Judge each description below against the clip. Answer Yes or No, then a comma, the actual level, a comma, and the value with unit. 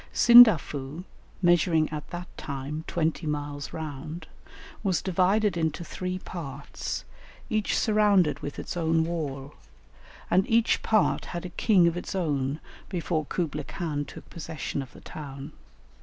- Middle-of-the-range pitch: Yes, medium, 165 Hz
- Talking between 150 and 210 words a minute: No, slow, 135 wpm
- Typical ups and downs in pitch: Yes, average, 3.6 semitones